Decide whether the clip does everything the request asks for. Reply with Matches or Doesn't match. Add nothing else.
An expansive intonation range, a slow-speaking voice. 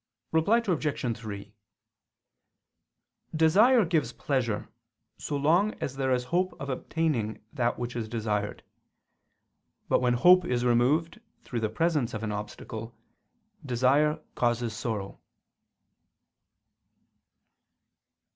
Matches